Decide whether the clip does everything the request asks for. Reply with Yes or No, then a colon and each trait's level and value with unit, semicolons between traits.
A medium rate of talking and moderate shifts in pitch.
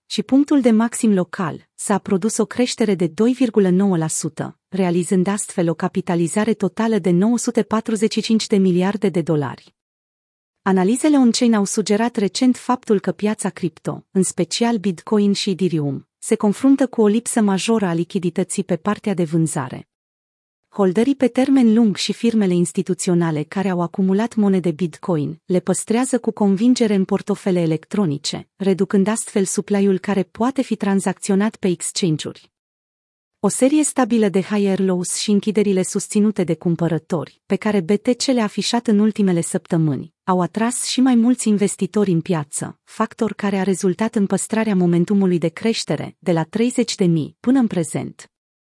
Yes: average, 145 wpm; average, 3.7 semitones